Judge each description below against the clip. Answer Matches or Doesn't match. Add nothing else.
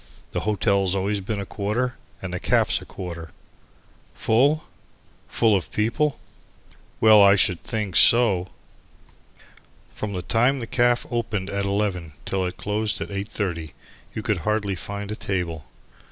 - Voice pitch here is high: Doesn't match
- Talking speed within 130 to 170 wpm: Matches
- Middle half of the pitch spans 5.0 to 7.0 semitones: Doesn't match